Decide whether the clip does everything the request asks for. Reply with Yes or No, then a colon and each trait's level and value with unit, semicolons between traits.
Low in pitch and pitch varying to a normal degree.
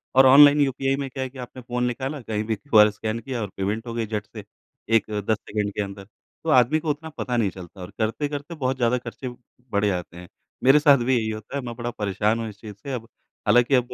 Yes: low, 120 Hz; average, 3.9 semitones